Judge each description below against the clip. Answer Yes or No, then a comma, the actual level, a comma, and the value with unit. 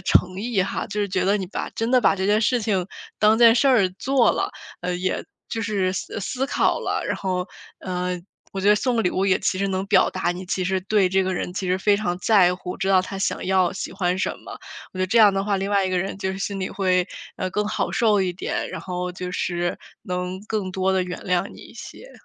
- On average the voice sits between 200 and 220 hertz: No, high, 190 Hz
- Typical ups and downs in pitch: No, narrow, 2.2 semitones